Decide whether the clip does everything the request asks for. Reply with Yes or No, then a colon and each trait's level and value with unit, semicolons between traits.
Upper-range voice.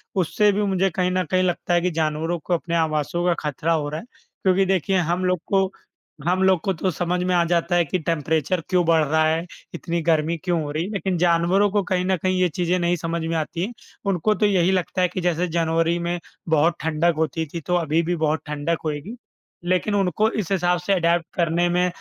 No: medium, 175 Hz